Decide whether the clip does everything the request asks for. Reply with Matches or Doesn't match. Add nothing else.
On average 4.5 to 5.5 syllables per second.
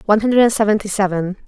Doesn't match